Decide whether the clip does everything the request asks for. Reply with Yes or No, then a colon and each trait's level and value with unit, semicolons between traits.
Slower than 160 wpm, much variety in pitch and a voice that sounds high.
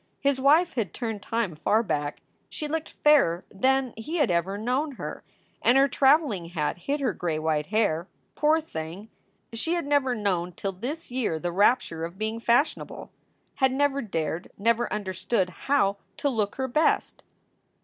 No: average, 165 wpm; wide, 7.3 semitones; high, 225 Hz